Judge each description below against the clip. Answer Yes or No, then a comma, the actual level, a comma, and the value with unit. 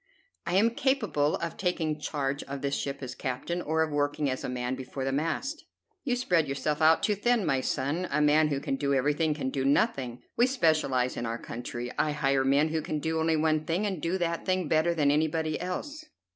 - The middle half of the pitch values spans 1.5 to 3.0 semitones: No, average, 3.7 semitones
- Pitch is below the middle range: No, medium, 155 Hz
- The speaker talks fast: Yes, fast, 215 wpm